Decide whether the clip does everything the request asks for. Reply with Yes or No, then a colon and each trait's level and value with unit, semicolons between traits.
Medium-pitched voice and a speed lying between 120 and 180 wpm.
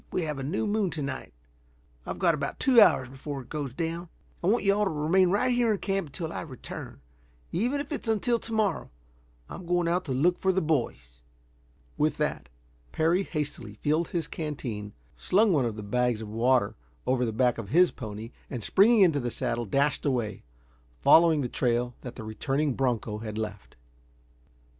No: medium, 150 Hz; average, 190 wpm